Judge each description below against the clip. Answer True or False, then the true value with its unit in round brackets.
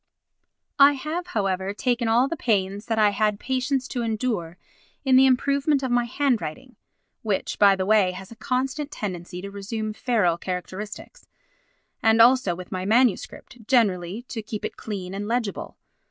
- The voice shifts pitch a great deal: False (4.6 semitones)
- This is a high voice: True (220 Hz)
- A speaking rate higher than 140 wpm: True (160 wpm)